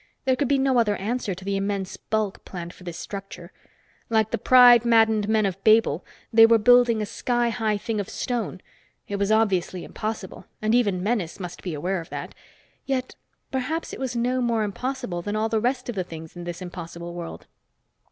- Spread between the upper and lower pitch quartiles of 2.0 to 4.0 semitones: No, average, 4.4 semitones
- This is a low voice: No, high, 215 Hz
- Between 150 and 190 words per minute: No, average, 200 wpm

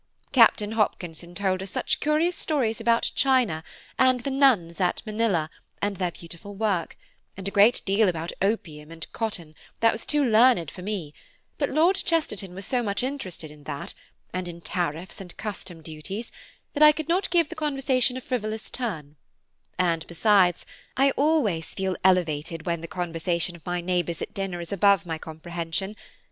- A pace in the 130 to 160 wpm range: No, average, 170 wpm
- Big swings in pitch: Yes, wide, 6.0 semitones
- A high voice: Yes, high, 195 Hz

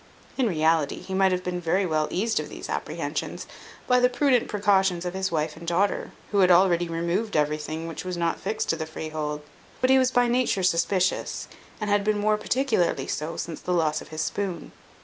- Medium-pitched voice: Yes, medium, 180 Hz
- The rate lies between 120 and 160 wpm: No, fast, 205 wpm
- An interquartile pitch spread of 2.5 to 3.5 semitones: No, average, 4.0 semitones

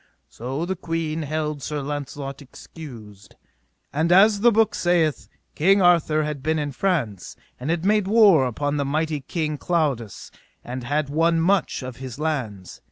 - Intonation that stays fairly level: No, average, 3.7 semitones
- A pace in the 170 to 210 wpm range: No, average, 160 wpm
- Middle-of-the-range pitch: Yes, medium, 150 Hz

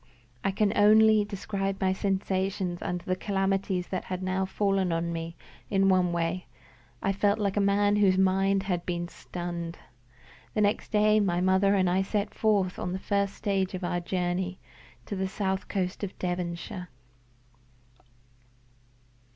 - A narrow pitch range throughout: Yes, narrow, 1.8 semitones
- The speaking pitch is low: No, high, 190 Hz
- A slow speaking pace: No, average, 155 wpm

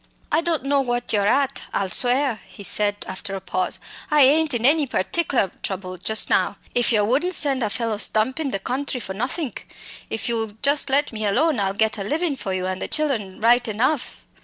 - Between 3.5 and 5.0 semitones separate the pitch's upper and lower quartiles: No, wide, 5.6 semitones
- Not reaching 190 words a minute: No, fast, 205 wpm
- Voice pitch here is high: Yes, high, 240 Hz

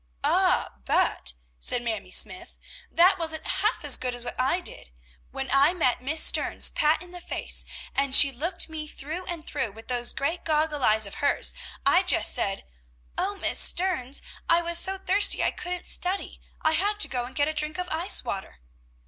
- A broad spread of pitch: Yes, wide, 5.7 semitones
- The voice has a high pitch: Yes, very high, 310 Hz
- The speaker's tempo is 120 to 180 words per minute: No, average, 190 wpm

